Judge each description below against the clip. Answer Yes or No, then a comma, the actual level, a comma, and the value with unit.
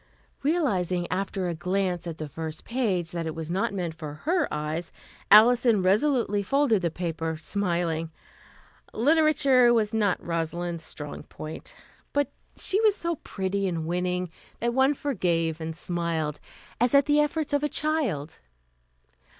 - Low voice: No, medium, 185 Hz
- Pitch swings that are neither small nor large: No, wide, 7.4 semitones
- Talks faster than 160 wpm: No, average, 145 wpm